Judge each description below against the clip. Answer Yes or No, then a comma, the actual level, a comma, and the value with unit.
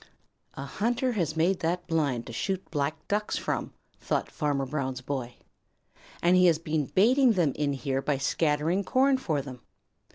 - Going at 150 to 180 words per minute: Yes, average, 165 wpm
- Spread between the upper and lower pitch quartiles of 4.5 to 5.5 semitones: Yes, average, 5.2 semitones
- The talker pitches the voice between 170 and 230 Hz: No, medium, 160 Hz